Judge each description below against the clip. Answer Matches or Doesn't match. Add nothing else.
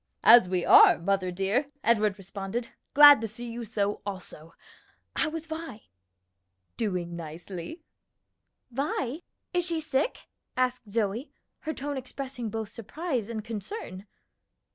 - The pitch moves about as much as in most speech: Doesn't match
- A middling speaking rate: Doesn't match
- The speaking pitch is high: Matches